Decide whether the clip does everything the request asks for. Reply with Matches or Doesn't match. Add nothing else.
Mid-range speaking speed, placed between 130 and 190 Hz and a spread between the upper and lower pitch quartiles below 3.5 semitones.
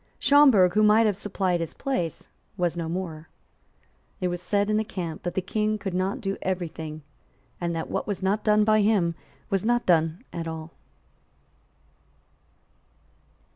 Doesn't match